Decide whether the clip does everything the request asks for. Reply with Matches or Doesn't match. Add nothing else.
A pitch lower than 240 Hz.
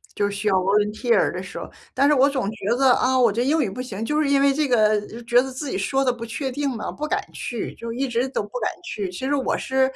Doesn't match